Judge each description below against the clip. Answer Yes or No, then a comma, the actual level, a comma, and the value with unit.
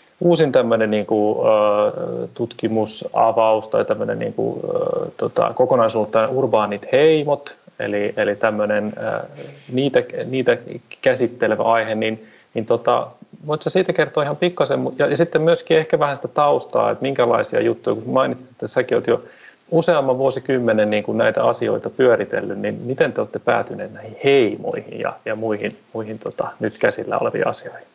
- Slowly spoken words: No, average, 135 wpm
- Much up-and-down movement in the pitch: Yes, wide, 7.5 semitones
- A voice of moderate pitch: No, low, 120 Hz